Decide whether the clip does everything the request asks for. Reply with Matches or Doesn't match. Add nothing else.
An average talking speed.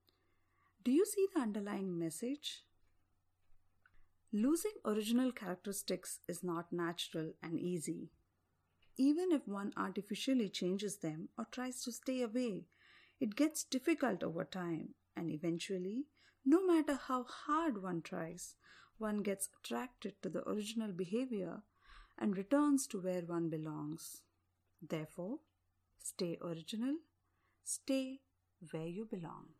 Doesn't match